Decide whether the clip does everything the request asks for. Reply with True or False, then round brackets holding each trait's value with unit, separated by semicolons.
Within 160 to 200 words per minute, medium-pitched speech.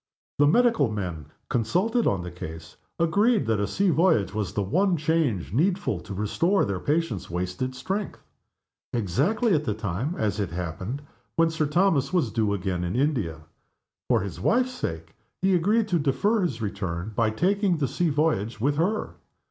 False (170 wpm; 130 Hz)